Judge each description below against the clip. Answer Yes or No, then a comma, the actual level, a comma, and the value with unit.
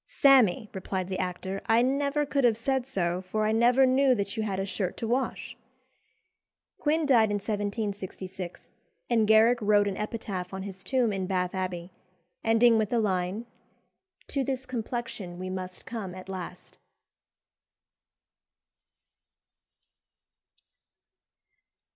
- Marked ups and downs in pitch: No, average, 4.2 semitones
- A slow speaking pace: Yes, slow, 130 wpm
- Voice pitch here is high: Yes, high, 210 Hz